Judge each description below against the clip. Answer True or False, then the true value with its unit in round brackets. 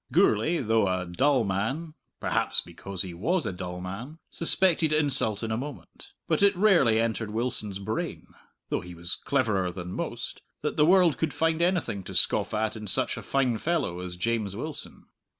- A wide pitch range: True (8.2 semitones)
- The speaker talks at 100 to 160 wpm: False (180 wpm)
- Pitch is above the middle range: False (115 Hz)